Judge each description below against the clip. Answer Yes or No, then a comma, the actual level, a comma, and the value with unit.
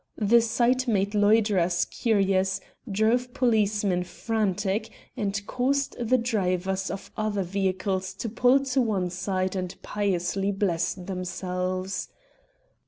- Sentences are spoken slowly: Yes, slow, 110 wpm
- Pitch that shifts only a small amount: No, average, 3.3 semitones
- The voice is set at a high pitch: Yes, high, 200 Hz